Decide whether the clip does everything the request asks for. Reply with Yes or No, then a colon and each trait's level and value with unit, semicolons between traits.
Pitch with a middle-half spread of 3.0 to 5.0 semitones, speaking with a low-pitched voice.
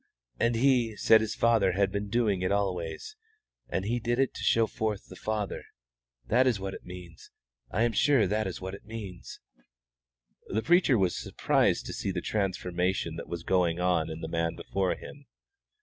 Yes: average, 3.9 semitones; low, 100 Hz